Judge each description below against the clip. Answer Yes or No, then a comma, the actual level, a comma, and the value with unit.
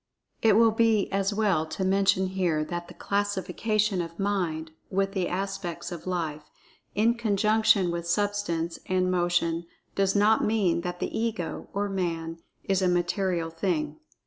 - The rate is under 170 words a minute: Yes, average, 150 wpm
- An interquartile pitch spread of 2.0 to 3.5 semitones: Yes, average, 3.0 semitones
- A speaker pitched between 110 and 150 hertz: No, high, 190 Hz